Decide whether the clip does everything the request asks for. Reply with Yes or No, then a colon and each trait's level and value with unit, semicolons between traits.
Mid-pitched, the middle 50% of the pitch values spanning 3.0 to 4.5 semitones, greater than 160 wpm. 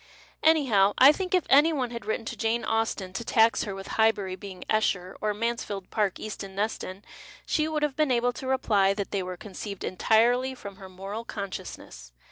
No: high, 220 Hz; average, 4.1 semitones; average, 190 wpm